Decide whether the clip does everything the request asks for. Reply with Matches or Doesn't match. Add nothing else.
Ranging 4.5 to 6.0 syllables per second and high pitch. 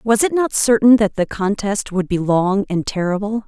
Matches